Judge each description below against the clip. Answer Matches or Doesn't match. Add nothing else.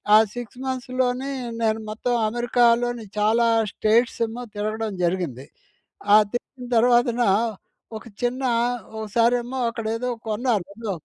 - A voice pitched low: Doesn't match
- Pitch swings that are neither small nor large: Doesn't match